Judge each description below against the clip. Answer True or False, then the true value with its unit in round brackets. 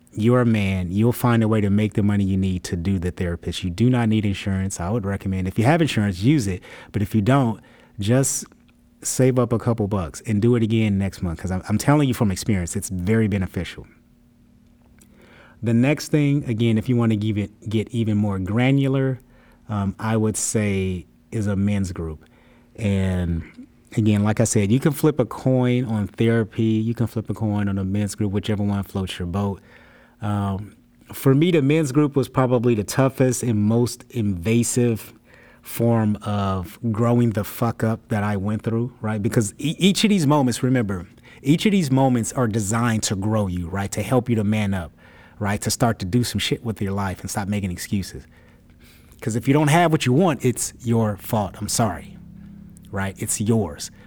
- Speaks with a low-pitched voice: True (110 Hz)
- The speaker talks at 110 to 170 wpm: False (200 wpm)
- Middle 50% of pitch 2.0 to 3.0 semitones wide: False (3.5 semitones)